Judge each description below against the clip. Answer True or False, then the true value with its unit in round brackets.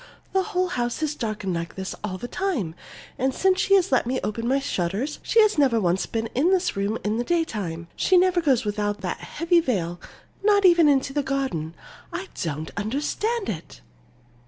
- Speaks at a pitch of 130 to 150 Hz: False (255 Hz)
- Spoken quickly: False (185 wpm)